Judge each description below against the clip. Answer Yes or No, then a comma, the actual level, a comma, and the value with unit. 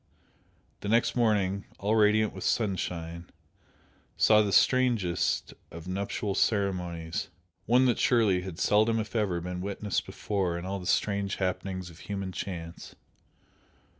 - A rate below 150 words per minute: Yes, slow, 135 wpm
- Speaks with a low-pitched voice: Yes, low, 100 Hz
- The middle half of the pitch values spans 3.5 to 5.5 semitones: No, average, 3.0 semitones